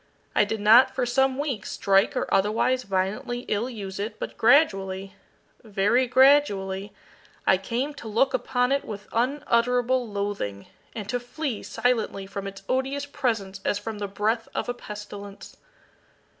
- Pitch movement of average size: Yes, average, 4.2 semitones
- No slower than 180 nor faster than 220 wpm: No, average, 150 wpm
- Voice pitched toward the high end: Yes, high, 225 Hz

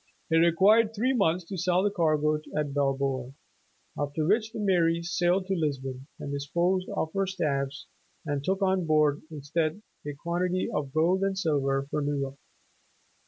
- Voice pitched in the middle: Yes, medium, 165 Hz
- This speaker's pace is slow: No, average, 165 wpm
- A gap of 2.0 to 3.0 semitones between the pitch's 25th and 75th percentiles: No, average, 4.6 semitones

